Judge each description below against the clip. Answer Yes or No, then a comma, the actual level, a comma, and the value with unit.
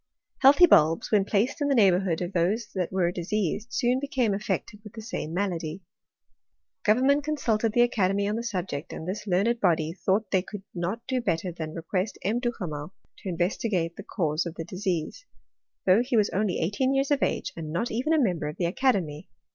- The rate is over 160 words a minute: Yes, average, 195 wpm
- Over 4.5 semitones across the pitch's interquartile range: Yes, average, 5.2 semitones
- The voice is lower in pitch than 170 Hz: No, high, 195 Hz